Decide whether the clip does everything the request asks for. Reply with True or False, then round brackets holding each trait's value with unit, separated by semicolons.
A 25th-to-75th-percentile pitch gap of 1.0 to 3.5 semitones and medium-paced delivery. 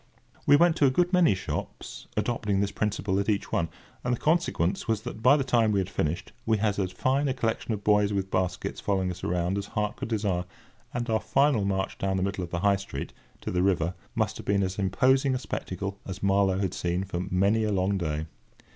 False (3.2 semitones; 225 wpm)